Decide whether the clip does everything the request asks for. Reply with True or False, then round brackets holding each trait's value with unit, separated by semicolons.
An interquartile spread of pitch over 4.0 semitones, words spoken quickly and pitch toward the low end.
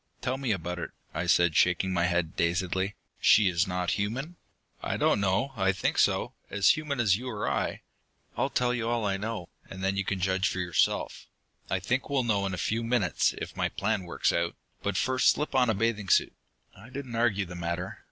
True (4.6 semitones; 210 wpm; 100 Hz)